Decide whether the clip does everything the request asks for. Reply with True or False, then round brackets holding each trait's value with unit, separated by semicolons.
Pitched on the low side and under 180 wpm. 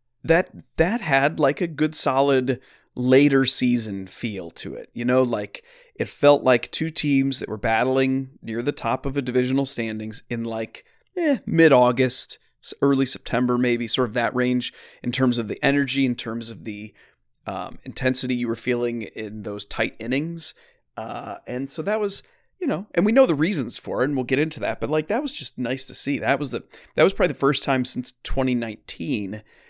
False (130 Hz; 200 wpm)